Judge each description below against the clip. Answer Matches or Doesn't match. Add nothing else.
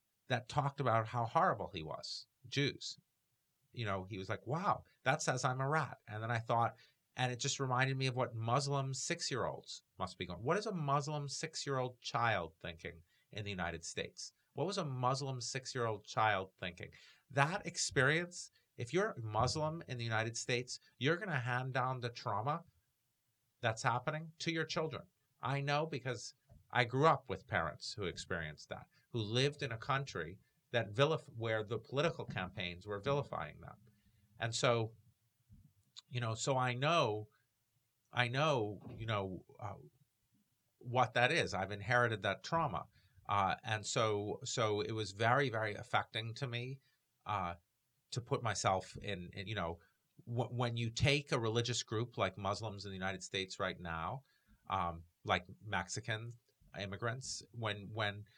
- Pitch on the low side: Matches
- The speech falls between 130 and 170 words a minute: Matches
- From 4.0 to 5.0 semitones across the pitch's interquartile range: Matches